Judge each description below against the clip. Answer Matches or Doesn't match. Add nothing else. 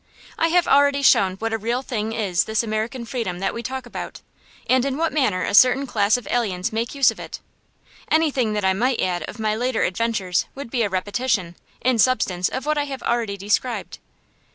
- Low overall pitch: Doesn't match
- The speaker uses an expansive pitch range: Doesn't match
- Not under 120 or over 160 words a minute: Doesn't match